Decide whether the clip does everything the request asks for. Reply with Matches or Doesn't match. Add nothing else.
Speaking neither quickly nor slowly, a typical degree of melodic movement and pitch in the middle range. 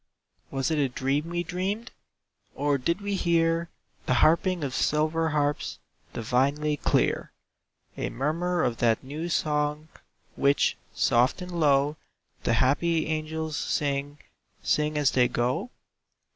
Doesn't match